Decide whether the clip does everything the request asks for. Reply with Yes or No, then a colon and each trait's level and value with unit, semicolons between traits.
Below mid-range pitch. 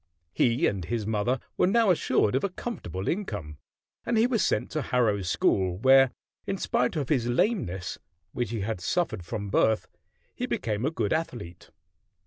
Yes: low, 120 Hz